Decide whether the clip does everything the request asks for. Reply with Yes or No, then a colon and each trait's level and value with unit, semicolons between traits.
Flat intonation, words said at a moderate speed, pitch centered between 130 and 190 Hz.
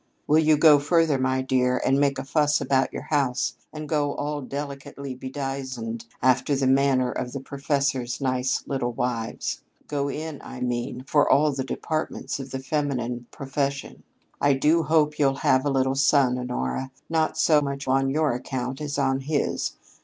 Yes: narrow, 2.0 semitones; average, 170 wpm; low, 135 Hz